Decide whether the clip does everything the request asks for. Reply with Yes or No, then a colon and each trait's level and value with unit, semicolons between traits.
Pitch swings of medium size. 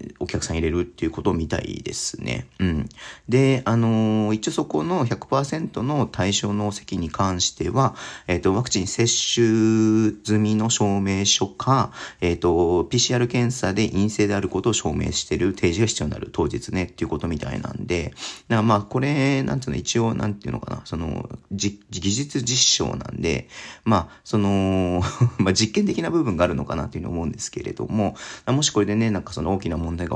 Yes: average, 3.7 semitones